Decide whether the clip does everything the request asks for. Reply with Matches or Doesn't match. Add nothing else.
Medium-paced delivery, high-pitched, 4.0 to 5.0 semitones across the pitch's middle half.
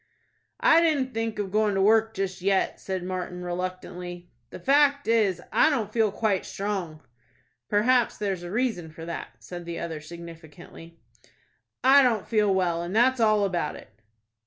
Matches